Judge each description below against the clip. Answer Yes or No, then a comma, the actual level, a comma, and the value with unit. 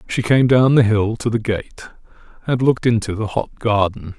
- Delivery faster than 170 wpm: Yes, average, 200 wpm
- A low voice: Yes, low, 110 Hz